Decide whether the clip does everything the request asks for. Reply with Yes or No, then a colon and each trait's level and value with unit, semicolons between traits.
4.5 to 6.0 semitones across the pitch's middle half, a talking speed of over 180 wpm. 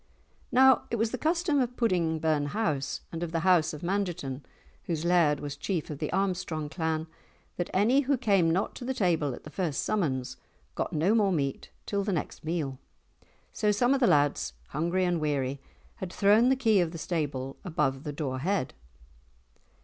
Yes: wide, 5.5 semitones; average, 190 wpm